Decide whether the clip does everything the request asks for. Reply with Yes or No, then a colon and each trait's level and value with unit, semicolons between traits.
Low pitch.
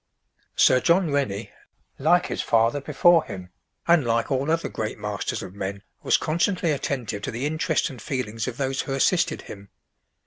Yes: low, 130 Hz